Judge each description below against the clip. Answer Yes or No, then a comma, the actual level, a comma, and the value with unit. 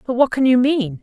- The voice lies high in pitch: Yes, high, 245 Hz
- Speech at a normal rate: No, fast, 295 wpm